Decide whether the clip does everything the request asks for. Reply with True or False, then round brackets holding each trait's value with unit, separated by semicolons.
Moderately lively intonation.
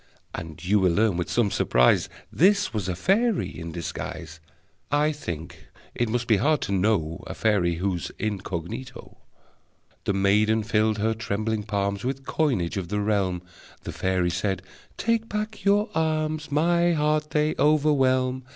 False (8.2 semitones)